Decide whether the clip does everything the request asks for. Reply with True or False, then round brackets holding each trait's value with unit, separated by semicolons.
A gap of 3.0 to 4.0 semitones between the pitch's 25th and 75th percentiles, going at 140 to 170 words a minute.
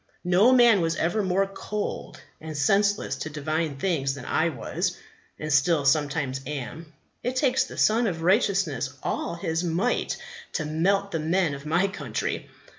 False (4.6 semitones; 160 wpm)